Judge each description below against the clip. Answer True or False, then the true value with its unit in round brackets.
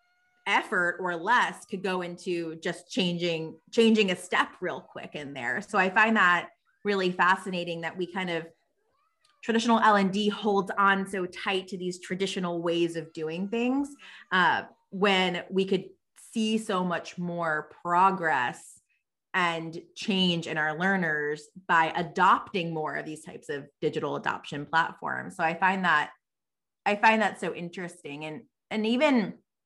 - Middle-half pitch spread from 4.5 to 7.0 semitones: False (3.4 semitones)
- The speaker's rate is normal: True (155 wpm)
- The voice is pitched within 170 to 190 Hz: True (185 Hz)